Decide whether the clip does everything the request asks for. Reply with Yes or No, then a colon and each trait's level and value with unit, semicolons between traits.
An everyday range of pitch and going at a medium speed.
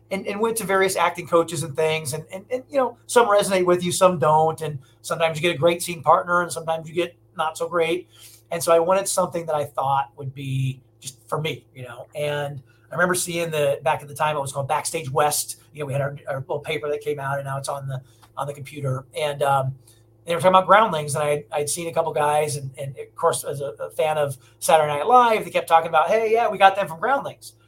No: average, 4.0 semitones; fast, 260 wpm